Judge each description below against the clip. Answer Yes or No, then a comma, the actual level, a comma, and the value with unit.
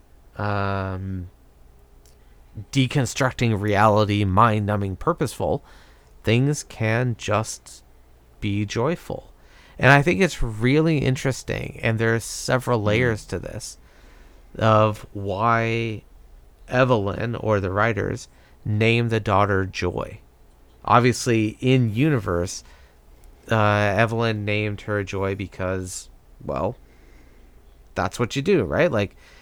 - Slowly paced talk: Yes, slow, 100 wpm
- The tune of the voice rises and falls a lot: Yes, wide, 6.3 semitones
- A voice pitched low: Yes, low, 105 Hz